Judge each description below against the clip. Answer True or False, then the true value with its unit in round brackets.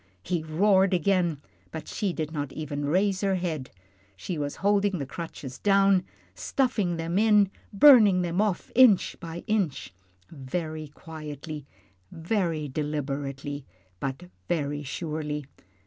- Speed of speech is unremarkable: False (125 wpm)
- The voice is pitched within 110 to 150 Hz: False (165 Hz)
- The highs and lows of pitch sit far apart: False (4.8 semitones)